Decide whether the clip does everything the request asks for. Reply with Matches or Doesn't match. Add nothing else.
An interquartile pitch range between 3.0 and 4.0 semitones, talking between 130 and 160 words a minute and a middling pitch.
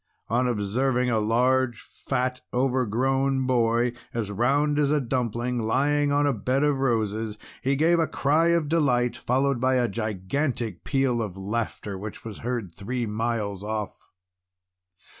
Doesn't match